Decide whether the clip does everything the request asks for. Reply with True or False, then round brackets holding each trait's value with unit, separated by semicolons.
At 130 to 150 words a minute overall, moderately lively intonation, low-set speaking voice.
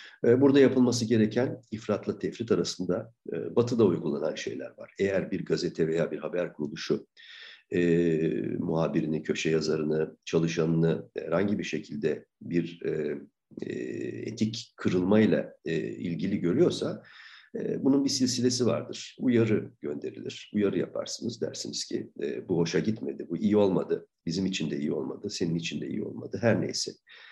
False (135 wpm; 6.5 semitones; 95 Hz)